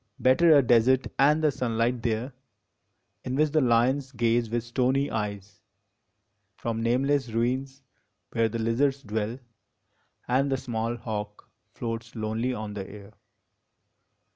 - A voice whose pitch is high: No, low, 120 Hz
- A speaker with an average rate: No, slow, 130 wpm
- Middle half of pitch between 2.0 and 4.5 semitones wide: Yes, average, 2.9 semitones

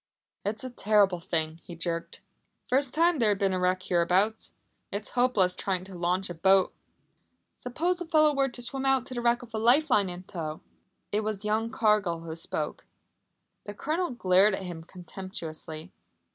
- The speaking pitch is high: Yes, high, 200 Hz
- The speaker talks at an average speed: Yes, average, 185 wpm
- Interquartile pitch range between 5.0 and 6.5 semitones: Yes, average, 5.3 semitones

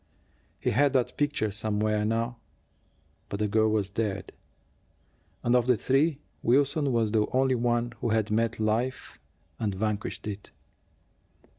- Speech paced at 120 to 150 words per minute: Yes, average, 140 wpm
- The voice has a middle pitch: No, low, 115 Hz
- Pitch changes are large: No, average, 2.8 semitones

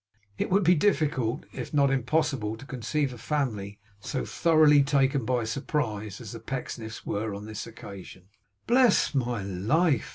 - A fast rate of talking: No, average, 155 wpm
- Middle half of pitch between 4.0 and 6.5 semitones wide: Yes, average, 5.2 semitones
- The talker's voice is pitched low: Yes, low, 130 Hz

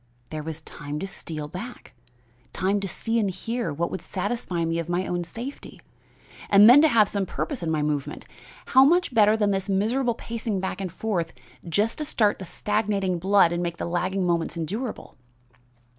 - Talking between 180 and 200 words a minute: Yes, average, 190 wpm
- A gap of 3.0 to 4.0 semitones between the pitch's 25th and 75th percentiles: No, average, 4.7 semitones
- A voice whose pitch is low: No, high, 195 Hz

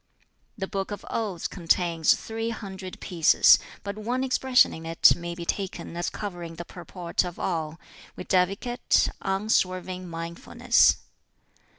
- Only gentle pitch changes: No, average, 3.1 semitones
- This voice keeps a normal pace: No, slow, 125 wpm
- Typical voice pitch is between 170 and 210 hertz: Yes, medium, 185 Hz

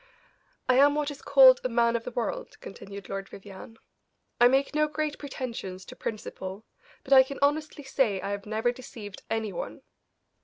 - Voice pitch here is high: Yes, high, 245 Hz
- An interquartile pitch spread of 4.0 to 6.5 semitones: Yes, average, 5.3 semitones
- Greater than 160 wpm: Yes, average, 180 wpm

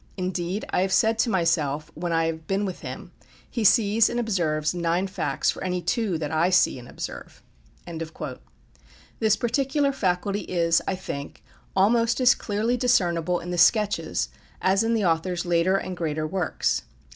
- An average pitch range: Yes, average, 4.3 semitones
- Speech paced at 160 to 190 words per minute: Yes, average, 165 wpm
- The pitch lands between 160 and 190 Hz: Yes, medium, 185 Hz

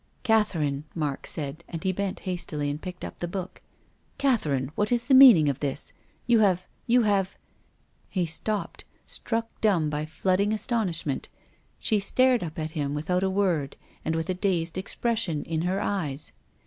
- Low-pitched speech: No, medium, 180 Hz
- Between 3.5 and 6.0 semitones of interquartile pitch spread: Yes, average, 5.2 semitones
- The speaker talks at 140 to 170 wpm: No, average, 180 wpm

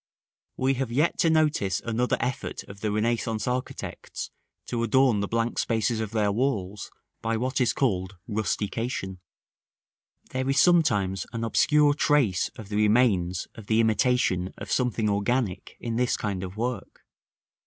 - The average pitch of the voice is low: Yes, low, 115 Hz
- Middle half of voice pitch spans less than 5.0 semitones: Yes, average, 3.8 semitones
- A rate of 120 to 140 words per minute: No, average, 155 wpm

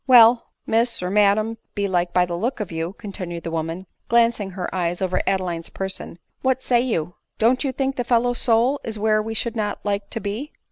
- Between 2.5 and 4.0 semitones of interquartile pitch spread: No, average, 4.4 semitones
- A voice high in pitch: Yes, high, 210 Hz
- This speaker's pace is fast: Yes, fast, 230 wpm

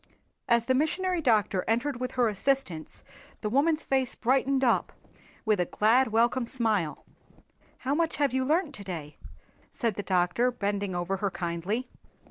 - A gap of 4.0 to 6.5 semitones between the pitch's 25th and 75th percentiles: Yes, average, 5.1 semitones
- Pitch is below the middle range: No, high, 235 Hz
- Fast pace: No, average, 155 wpm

